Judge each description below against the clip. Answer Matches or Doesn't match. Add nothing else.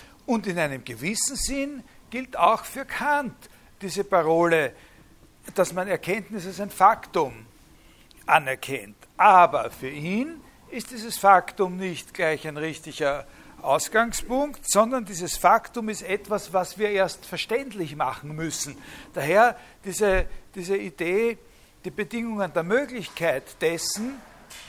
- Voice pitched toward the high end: Matches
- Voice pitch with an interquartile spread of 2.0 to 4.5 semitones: Doesn't match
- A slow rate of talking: Matches